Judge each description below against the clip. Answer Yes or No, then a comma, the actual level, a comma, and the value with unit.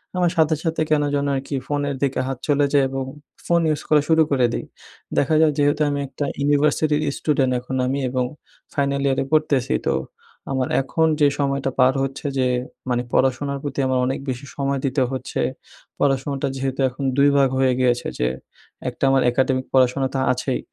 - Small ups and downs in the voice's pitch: Yes, narrow, 1.7 semitones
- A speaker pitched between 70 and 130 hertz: No, medium, 140 Hz